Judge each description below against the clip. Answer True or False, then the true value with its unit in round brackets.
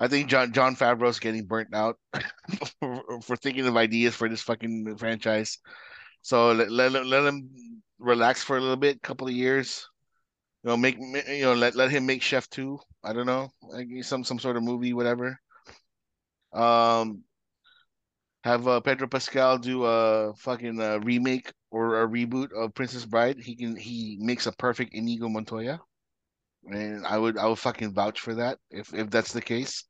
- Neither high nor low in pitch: False (120 Hz)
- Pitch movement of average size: False (2.3 semitones)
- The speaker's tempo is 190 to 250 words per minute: False (180 wpm)